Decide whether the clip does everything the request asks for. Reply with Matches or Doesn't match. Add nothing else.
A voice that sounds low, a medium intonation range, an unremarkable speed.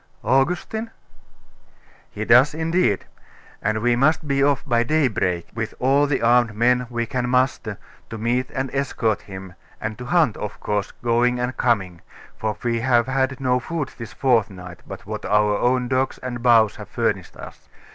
Matches